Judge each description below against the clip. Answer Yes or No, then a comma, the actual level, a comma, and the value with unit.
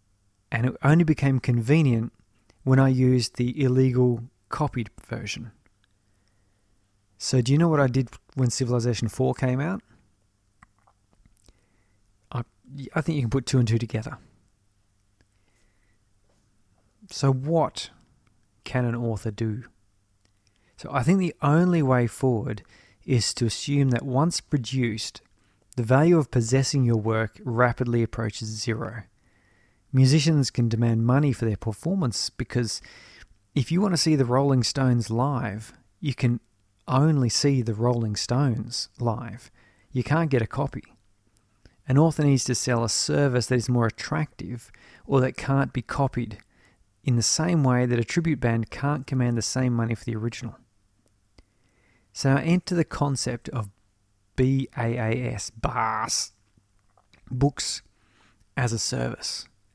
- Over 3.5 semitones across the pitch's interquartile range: Yes, average, 4.2 semitones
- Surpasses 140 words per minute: No, slow, 135 wpm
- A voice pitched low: Yes, low, 120 Hz